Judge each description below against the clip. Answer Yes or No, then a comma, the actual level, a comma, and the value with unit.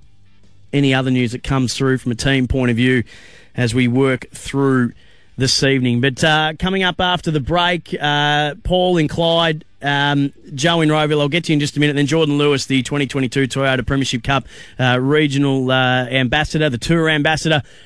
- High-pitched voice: No, medium, 140 Hz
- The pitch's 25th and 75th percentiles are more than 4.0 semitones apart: No, average, 3.3 semitones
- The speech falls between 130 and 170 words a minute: No, average, 190 wpm